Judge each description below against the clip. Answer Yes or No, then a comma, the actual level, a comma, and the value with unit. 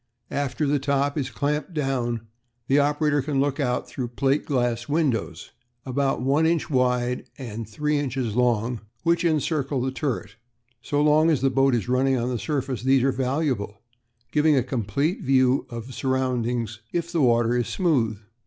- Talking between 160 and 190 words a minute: Yes, average, 170 wpm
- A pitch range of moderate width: Yes, average, 3.1 semitones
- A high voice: No, low, 135 Hz